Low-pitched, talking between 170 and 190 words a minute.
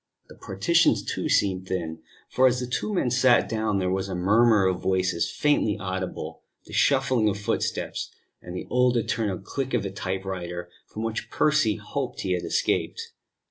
Yes: low, 105 Hz; average, 175 wpm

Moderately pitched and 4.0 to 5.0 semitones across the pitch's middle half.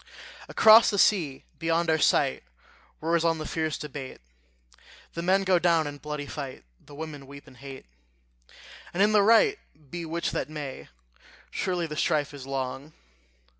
No: medium, 155 Hz; average, 3.2 semitones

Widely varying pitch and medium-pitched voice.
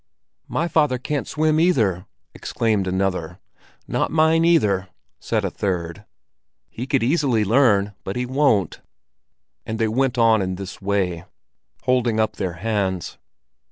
No: wide, 5.9 semitones; low, 110 Hz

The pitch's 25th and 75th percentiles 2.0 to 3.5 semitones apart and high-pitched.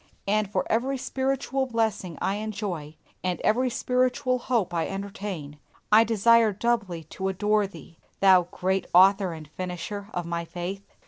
No: average, 4.2 semitones; high, 200 Hz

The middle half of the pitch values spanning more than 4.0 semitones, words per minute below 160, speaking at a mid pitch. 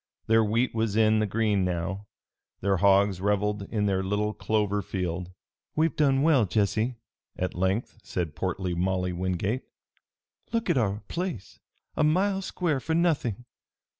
No: average, 4.6 semitones; average, 145 wpm; low, 105 Hz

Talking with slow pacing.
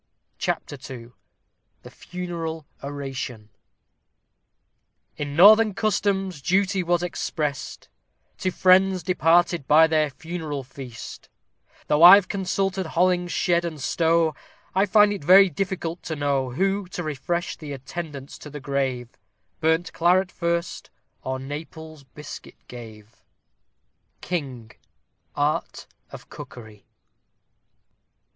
Yes: slow, 105 wpm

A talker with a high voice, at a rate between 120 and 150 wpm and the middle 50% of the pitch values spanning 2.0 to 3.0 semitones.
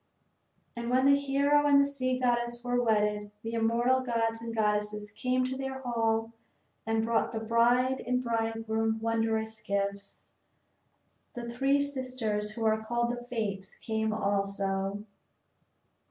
Yes: high, 230 Hz; average, 140 wpm; narrow, 2.5 semitones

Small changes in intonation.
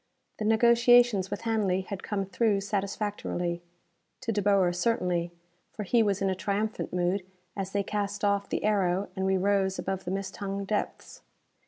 Yes: narrow, 1.8 semitones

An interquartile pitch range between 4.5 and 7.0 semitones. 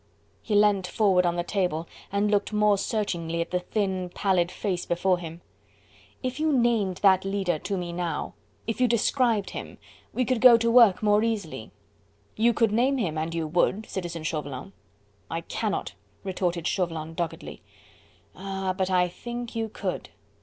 No: average, 4.0 semitones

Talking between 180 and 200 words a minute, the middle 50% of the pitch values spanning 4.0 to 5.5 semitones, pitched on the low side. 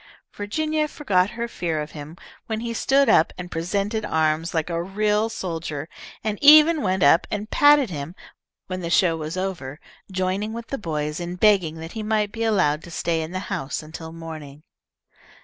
No: average, 185 wpm; average, 5.0 semitones; medium, 185 Hz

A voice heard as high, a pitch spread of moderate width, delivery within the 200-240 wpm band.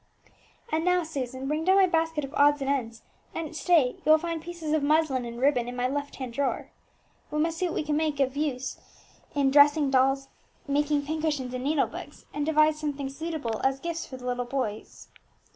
Yes: very high, 290 Hz; average, 3.0 semitones; fast, 205 wpm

